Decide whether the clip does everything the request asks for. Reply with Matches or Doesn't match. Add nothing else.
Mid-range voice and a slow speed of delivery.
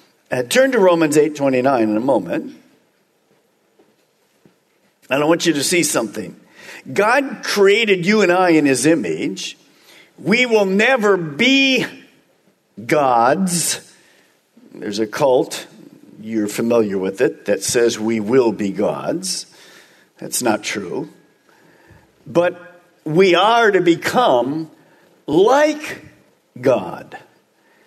Matches